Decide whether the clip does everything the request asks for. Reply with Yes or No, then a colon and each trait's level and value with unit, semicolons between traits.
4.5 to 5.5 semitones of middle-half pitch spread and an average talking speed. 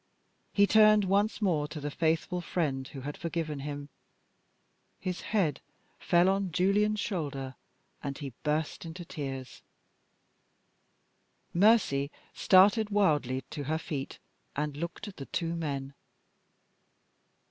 No: average, 5.1 semitones; slow, 120 wpm